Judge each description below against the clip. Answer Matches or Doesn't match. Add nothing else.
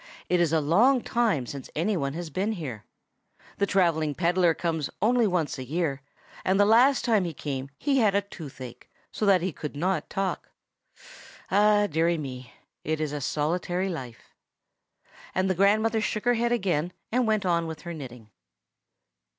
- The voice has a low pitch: Doesn't match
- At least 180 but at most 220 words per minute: Doesn't match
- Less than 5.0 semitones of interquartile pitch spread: Doesn't match